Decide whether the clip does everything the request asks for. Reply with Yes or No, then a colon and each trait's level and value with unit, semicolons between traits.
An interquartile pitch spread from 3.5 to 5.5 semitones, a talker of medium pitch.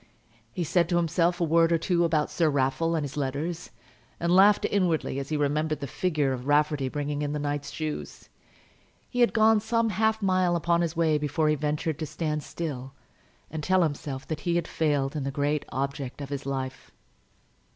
No: average, 3.1 semitones; medium, 155 Hz